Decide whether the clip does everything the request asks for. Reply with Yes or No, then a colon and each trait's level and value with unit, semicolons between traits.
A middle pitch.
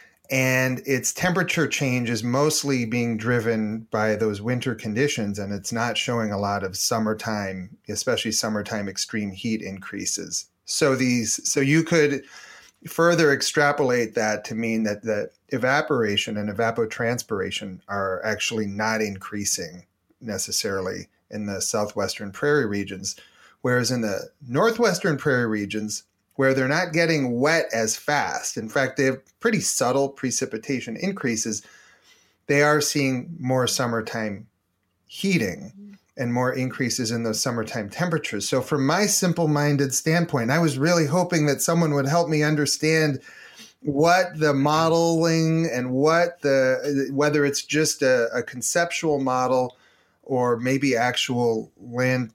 No: low, 130 Hz